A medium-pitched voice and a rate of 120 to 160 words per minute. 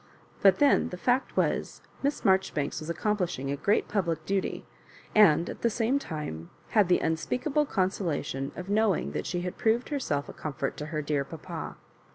No: medium, 180 Hz; average, 180 wpm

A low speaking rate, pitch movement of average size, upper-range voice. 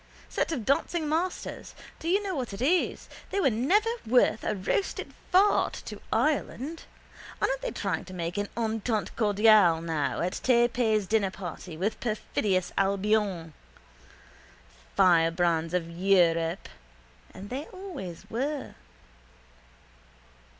No: slow, 120 wpm; wide, 7.4 semitones; high, 215 Hz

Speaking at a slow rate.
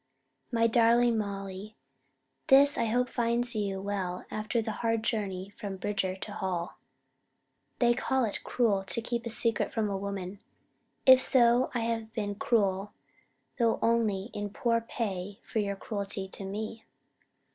No: average, 150 wpm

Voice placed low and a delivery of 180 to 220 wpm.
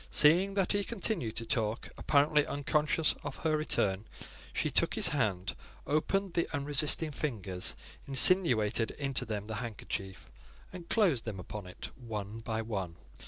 No: low, 130 Hz; average, 145 wpm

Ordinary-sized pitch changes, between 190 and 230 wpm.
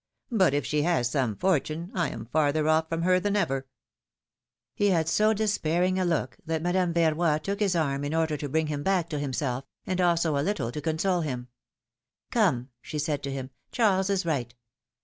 Yes: average, 4.2 semitones; average, 200 wpm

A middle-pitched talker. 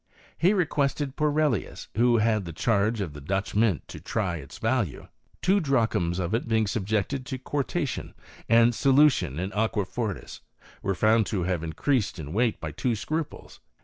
No: low, 110 Hz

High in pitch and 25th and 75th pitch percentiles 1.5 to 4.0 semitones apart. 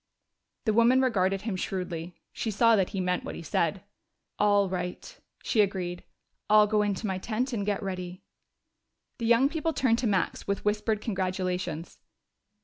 Yes: high, 200 Hz; average, 3.4 semitones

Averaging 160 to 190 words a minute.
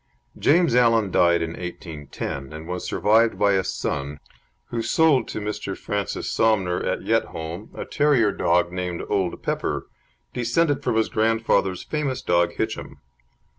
No: average, 140 wpm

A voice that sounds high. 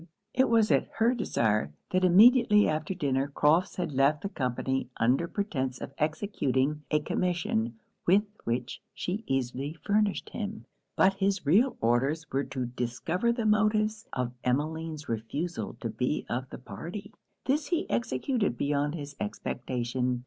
No: medium, 155 Hz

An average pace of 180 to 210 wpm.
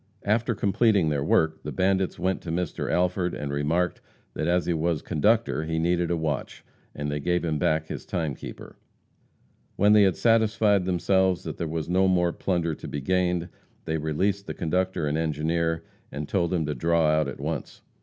Yes: average, 185 wpm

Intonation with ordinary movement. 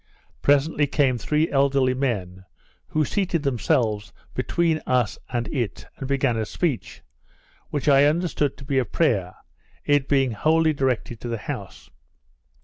Yes: average, 3.8 semitones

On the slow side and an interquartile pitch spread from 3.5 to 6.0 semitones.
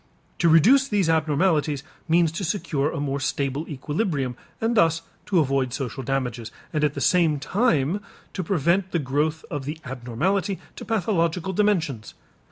No: average, 155 wpm; average, 5.0 semitones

